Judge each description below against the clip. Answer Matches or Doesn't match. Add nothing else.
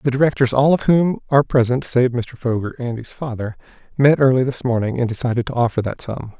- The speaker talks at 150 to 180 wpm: Doesn't match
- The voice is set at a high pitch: Doesn't match